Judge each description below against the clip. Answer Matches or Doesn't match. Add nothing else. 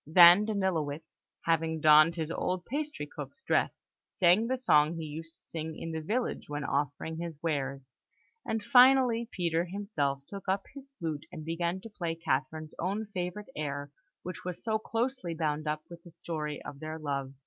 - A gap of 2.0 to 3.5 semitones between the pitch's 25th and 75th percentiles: Doesn't match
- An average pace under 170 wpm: Doesn't match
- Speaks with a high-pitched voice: Doesn't match